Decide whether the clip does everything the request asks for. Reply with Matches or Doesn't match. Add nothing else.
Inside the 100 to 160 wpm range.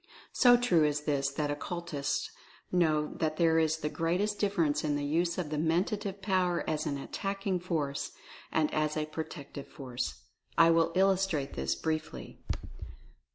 Matches